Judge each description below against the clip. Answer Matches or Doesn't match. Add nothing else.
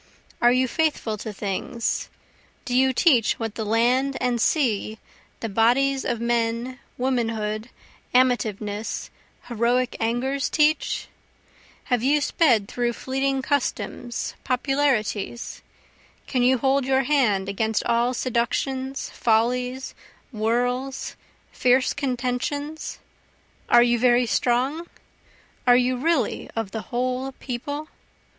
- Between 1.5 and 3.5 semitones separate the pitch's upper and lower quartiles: Matches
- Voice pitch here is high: Matches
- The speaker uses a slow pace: Matches